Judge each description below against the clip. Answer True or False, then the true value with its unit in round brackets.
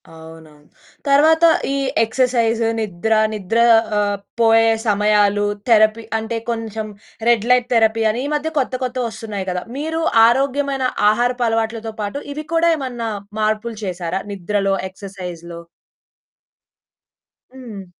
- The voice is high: True (225 Hz)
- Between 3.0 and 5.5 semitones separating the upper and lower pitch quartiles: True (3.5 semitones)